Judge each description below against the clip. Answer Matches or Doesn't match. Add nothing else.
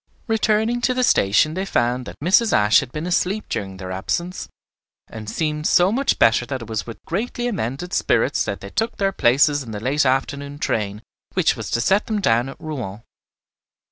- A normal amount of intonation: Doesn't match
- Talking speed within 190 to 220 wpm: Matches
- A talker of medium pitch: Matches